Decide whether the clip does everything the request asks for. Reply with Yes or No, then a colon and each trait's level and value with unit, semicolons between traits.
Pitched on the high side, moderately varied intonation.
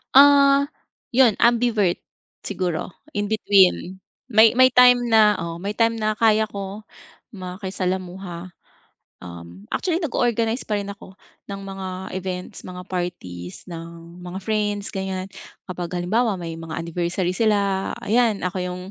Yes: high, 195 Hz; average, 3.5 semitones